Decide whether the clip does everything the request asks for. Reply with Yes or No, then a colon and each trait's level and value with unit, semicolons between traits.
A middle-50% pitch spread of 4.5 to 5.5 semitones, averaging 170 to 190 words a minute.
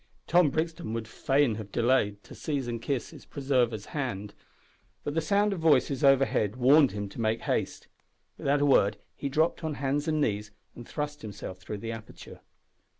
Yes: average, 5.1 semitones; average, 180 wpm